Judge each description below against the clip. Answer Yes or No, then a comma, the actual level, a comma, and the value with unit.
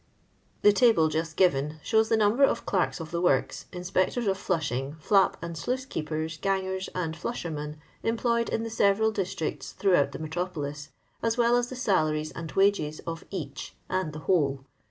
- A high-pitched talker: No, medium, 180 Hz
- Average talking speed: Yes, average, 175 wpm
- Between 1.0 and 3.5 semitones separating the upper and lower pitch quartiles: No, average, 5.0 semitones